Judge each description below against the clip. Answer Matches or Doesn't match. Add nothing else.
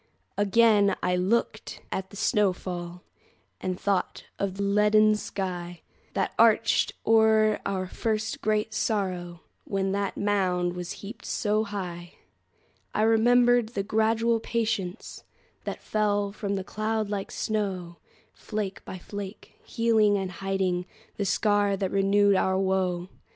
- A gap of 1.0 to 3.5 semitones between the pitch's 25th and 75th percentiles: Matches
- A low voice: Doesn't match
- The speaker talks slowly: Matches